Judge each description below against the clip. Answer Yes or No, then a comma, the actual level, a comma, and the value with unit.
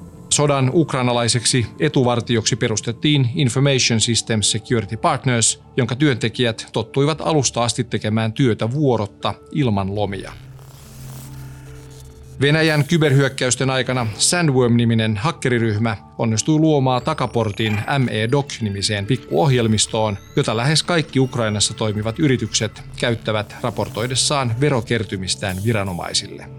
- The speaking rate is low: Yes, slow, 85 wpm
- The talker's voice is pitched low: Yes, low, 120 Hz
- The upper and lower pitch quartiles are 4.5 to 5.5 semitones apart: No, average, 3.7 semitones